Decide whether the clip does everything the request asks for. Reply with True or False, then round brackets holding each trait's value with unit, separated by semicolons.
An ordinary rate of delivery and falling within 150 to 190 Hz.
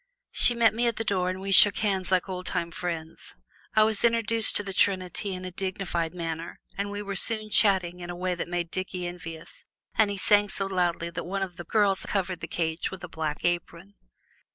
False (220 wpm; 185 Hz)